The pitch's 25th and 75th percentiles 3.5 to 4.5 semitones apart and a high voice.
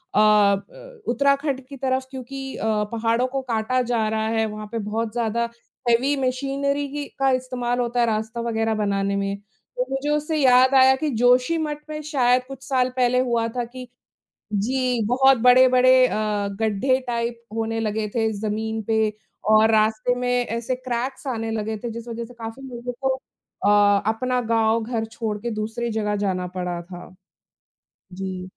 No: average, 2.8 semitones; high, 235 Hz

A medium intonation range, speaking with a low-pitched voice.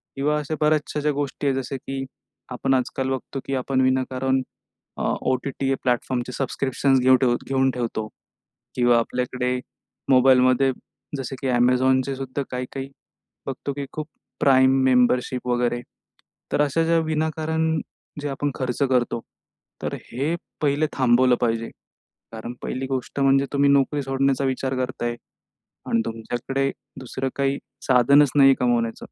No: narrow, 1.7 semitones; low, 130 Hz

